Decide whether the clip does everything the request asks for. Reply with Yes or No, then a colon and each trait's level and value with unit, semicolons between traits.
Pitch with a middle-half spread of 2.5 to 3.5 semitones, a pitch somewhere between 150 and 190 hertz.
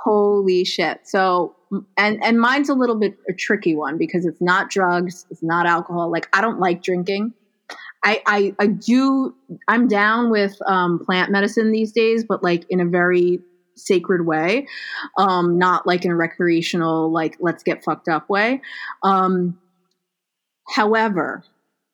Yes: average, 2.9 semitones; medium, 185 Hz